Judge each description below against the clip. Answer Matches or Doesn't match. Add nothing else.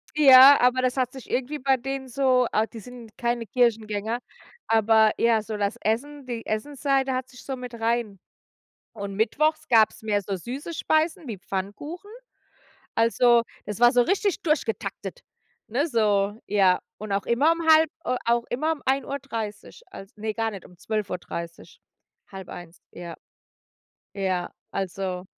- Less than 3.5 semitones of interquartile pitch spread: Doesn't match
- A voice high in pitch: Matches